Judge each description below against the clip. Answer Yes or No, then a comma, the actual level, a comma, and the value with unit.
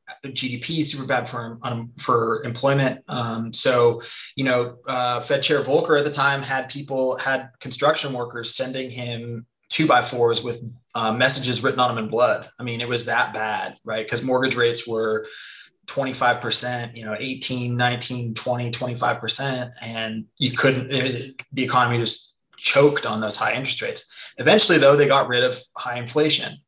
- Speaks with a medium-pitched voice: No, low, 125 Hz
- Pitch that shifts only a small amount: Yes, narrow, 2.1 semitones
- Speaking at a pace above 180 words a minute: No, average, 170 wpm